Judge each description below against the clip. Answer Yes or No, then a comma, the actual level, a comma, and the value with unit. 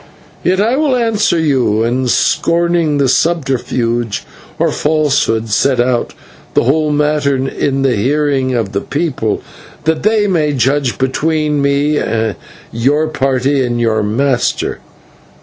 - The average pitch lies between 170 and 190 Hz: No, medium, 140 Hz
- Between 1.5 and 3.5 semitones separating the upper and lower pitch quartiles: No, average, 3.9 semitones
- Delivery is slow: Yes, slow, 125 wpm